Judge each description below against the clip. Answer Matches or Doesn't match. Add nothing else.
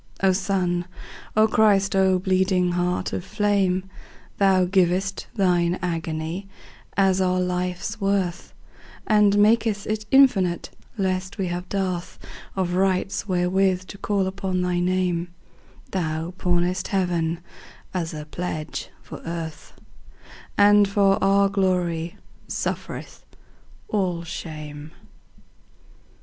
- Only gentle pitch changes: Matches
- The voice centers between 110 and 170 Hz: Doesn't match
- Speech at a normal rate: Doesn't match